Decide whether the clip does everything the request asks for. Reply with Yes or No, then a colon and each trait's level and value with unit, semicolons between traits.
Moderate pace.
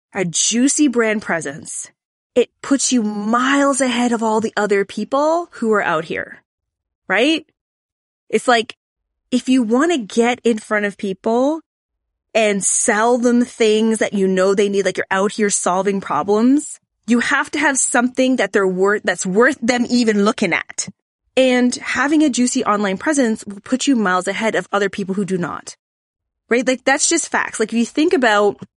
Yes: average, 180 wpm